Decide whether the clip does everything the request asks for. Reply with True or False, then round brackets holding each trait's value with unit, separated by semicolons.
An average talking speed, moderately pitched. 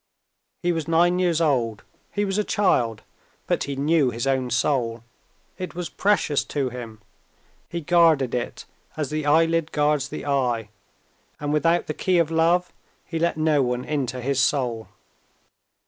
True (160 wpm; 150 Hz)